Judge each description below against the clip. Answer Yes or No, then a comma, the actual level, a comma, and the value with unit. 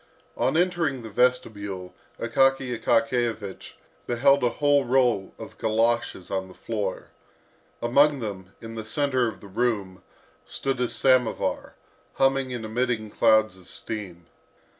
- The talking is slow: Yes, slow, 130 wpm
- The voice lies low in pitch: Yes, low, 115 Hz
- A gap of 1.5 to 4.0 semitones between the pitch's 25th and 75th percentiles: Yes, average, 3.7 semitones